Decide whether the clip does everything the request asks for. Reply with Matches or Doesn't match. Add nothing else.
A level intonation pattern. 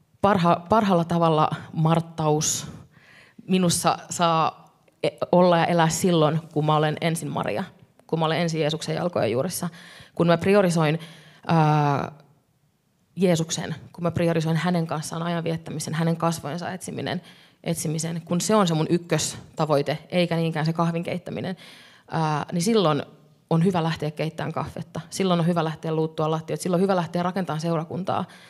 Matches